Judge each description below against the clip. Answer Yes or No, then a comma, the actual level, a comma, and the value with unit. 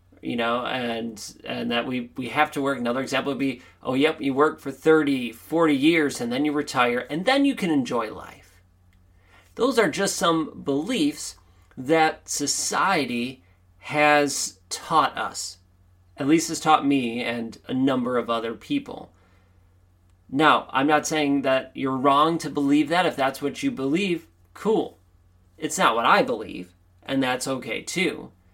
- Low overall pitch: Yes, low, 130 Hz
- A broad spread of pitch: Yes, wide, 8.2 semitones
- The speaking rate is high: No, average, 165 wpm